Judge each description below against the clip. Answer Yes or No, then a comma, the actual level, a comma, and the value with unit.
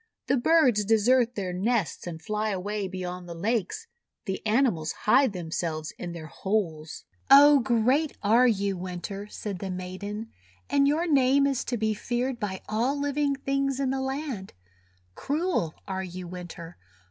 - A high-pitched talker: Yes, high, 215 Hz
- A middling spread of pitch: No, wide, 6.4 semitones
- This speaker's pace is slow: No, average, 155 wpm